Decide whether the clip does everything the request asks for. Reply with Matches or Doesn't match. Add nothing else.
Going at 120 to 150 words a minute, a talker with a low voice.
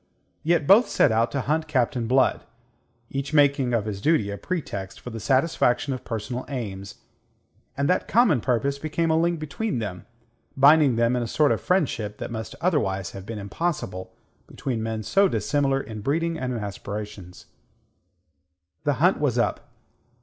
Doesn't match